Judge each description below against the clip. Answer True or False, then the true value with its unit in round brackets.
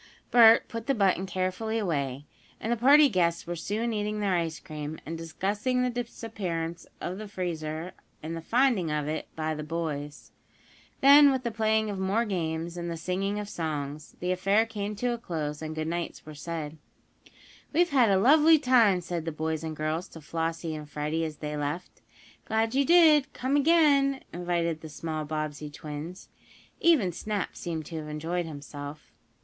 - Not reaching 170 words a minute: False (175 wpm)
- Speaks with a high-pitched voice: False (175 Hz)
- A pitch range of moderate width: False (6.0 semitones)